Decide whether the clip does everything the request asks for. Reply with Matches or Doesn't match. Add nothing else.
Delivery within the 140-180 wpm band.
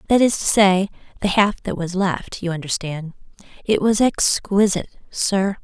Matches